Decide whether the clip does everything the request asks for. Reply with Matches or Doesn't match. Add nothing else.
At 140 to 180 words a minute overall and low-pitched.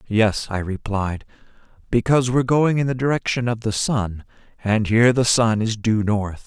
Matches